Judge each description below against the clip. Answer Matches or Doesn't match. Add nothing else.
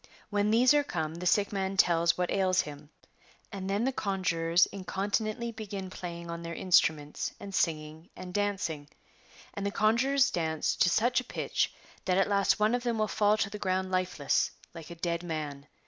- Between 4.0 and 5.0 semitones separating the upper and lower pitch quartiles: Doesn't match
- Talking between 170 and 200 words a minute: Matches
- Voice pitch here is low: Doesn't match